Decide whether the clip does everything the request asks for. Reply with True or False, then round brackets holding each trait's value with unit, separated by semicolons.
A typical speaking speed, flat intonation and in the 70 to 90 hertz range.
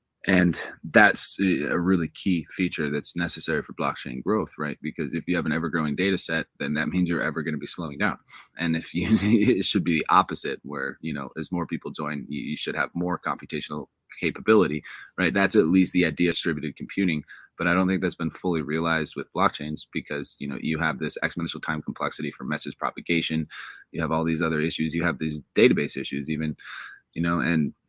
False (210 wpm; 2.2 semitones; 85 Hz)